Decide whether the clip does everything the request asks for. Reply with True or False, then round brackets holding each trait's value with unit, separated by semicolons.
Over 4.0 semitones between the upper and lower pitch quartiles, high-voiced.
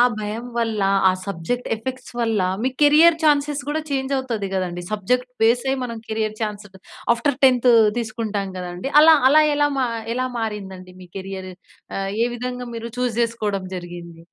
True (4.6 semitones; 230 Hz)